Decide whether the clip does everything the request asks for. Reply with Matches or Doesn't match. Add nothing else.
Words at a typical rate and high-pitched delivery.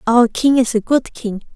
Doesn't match